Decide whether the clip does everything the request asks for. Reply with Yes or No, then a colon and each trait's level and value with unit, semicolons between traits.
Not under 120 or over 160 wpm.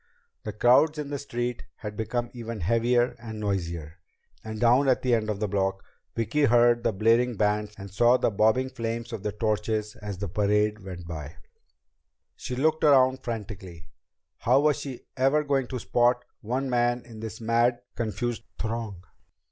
No: average, 170 wpm